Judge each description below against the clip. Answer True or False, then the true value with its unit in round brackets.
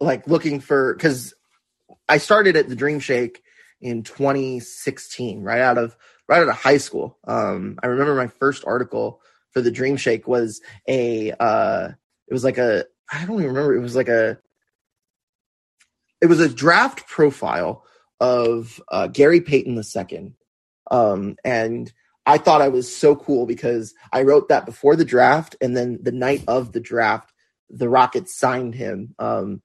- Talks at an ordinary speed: True (170 wpm)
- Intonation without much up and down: False (3.2 semitones)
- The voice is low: True (130 Hz)